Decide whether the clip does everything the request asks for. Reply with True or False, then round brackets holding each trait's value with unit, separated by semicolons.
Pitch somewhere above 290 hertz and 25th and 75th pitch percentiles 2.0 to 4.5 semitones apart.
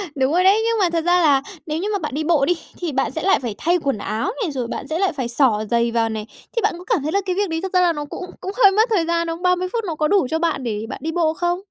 False (330 Hz; 4.9 semitones)